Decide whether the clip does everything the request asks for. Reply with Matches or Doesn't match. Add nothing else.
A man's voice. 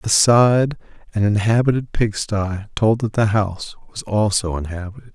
Matches